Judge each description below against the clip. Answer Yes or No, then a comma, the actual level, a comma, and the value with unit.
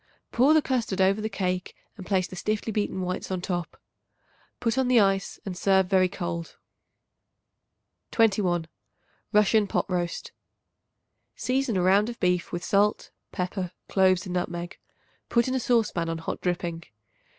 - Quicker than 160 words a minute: No, average, 150 wpm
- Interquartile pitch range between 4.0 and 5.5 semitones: No, average, 3.3 semitones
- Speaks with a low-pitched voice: No, high, 190 Hz